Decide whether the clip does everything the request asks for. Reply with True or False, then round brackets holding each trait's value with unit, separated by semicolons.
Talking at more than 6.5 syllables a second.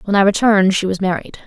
True (7.0 syllables/s)